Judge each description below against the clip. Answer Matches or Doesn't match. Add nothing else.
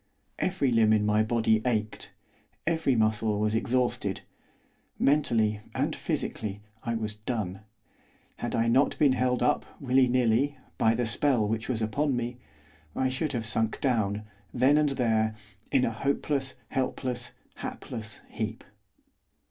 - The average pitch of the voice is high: Doesn't match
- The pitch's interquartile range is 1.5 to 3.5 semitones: Matches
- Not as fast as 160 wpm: Matches